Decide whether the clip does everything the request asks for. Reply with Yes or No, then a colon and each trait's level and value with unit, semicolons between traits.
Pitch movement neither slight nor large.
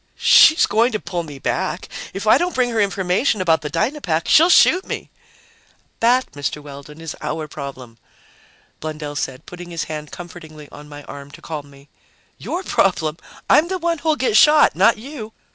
No: wide, 8.4 semitones